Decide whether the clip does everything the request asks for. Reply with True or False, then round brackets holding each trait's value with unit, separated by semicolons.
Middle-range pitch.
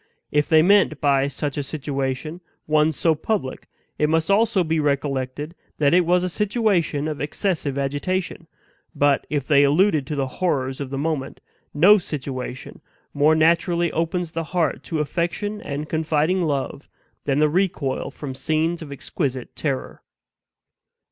True (155 Hz)